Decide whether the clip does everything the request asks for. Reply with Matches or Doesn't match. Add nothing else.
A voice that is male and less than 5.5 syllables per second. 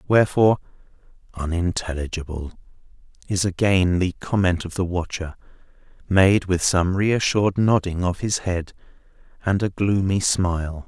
Matches